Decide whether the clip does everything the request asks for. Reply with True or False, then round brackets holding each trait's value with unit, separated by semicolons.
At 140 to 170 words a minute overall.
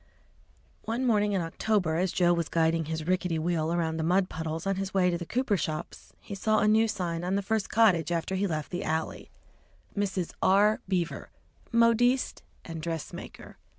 False (185 wpm)